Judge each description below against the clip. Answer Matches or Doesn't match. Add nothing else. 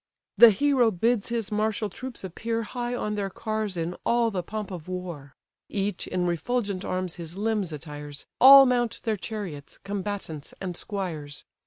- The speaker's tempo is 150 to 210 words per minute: Matches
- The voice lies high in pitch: Matches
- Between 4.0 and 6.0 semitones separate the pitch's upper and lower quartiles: Matches